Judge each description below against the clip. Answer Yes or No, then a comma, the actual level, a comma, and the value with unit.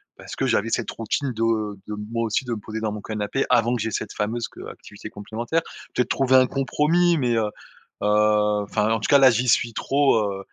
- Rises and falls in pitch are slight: No, average, 3.4 semitones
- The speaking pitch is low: Yes, low, 115 Hz